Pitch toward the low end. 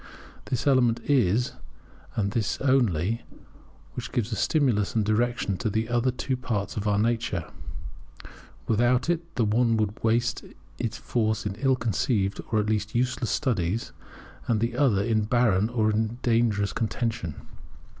Yes: low, 115 Hz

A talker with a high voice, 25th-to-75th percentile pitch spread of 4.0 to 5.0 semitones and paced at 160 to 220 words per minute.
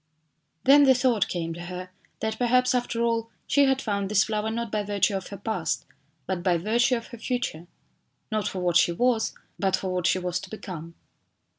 Yes: high, 210 Hz; average, 4.5 semitones; average, 200 wpm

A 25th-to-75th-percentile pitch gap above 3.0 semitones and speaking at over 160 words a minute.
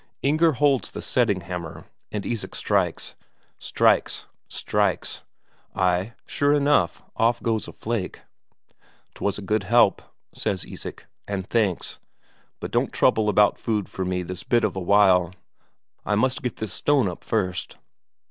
No: average, 4.3 semitones; average, 145 wpm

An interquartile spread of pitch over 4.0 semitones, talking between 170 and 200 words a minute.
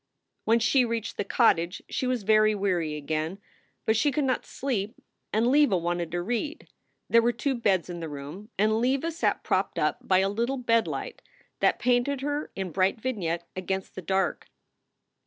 Yes: average, 5.0 semitones; average, 180 wpm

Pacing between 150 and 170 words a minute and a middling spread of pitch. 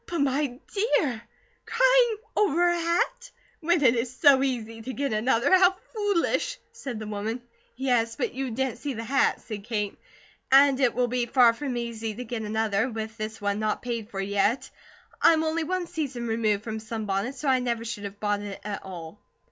No: average, 190 wpm; average, 4.6 semitones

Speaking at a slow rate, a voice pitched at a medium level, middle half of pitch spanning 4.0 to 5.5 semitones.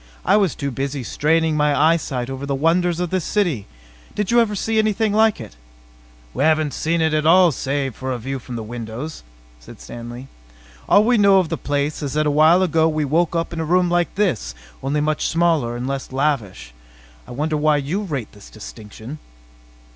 No: average, 200 wpm; medium, 150 Hz; average, 4.5 semitones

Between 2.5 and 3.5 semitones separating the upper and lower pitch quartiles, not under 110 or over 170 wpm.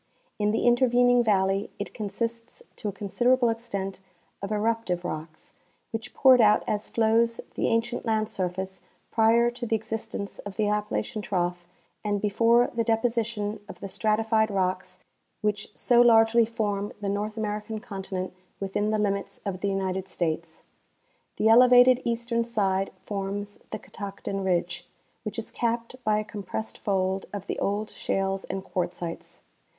Yes: average, 2.9 semitones; average, 155 wpm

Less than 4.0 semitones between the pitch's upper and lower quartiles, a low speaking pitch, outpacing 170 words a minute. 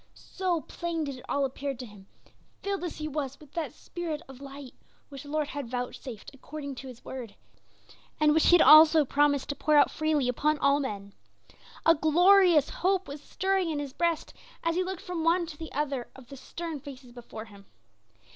No: average, 3.6 semitones; very high, 295 Hz; average, 200 wpm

